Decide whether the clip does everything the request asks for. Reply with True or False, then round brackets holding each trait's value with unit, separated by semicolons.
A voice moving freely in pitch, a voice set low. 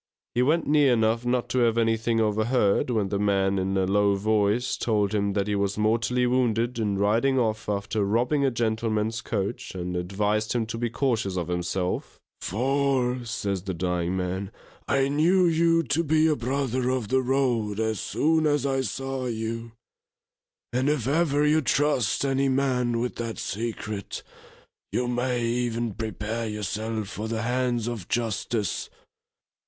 False (3.8 semitones; 115 Hz)